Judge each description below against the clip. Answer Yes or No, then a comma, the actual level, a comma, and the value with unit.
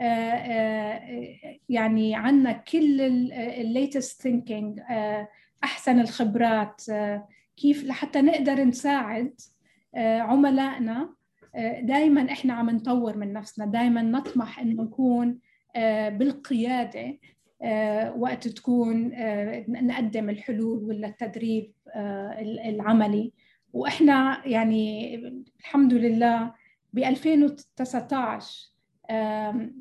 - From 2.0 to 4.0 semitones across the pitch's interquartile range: Yes, average, 3.0 semitones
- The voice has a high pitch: Yes, high, 235 Hz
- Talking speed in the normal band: Yes, average, 95 wpm